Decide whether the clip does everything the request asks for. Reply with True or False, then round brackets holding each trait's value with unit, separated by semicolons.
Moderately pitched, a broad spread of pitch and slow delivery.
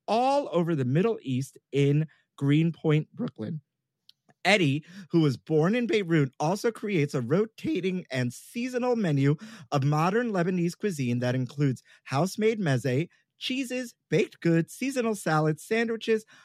True (170 Hz; 7.3 semitones; 130 wpm)